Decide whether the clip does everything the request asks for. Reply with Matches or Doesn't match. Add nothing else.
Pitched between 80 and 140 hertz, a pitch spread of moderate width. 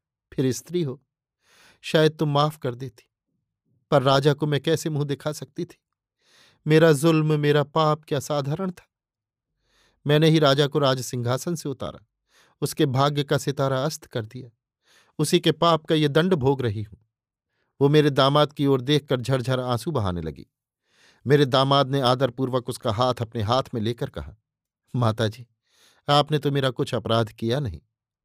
Matches